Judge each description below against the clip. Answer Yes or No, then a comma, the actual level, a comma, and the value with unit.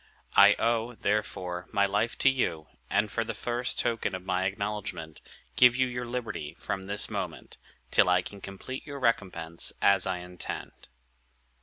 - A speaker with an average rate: Yes, average, 160 wpm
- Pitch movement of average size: Yes, average, 4.5 semitones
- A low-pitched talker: Yes, low, 100 Hz